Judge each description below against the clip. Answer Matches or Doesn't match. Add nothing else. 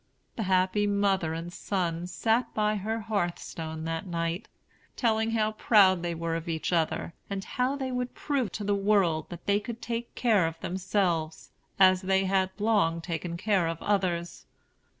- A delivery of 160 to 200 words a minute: Matches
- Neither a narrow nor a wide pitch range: Matches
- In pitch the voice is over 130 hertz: Matches